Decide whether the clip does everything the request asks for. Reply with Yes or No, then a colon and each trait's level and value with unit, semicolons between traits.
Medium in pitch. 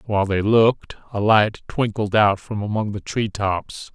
No: low, 105 Hz